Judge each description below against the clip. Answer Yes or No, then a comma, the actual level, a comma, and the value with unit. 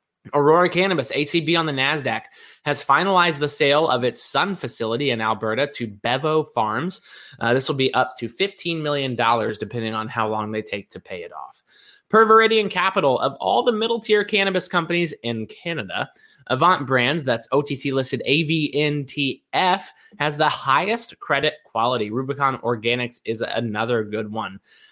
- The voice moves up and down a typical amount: No, wide, 6.1 semitones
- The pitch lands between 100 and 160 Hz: Yes, medium, 140 Hz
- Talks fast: No, average, 160 wpm